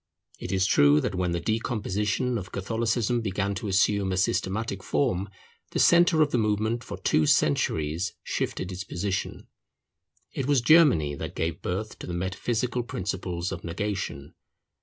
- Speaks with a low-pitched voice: Yes, low, 100 Hz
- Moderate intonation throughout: Yes, average, 4.2 semitones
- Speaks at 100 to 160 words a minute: Yes, average, 155 wpm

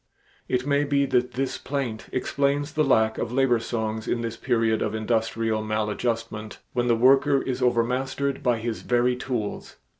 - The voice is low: Yes, low, 120 Hz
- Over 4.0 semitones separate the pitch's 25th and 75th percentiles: No, average, 3.1 semitones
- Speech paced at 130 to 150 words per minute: No, average, 160 wpm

